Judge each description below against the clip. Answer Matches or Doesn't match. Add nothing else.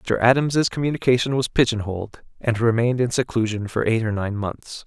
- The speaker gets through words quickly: Doesn't match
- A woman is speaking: Doesn't match